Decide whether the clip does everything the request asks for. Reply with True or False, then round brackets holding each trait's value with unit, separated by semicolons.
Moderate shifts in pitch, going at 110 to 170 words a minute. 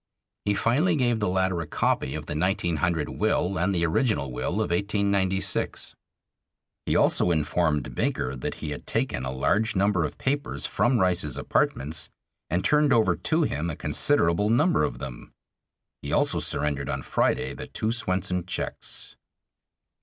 False (5.9 semitones; 155 wpm)